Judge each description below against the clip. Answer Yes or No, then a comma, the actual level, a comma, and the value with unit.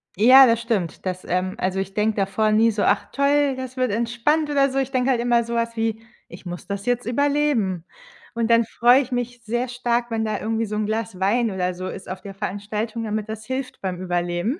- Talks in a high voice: Yes, high, 225 Hz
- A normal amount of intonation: Yes, average, 3.6 semitones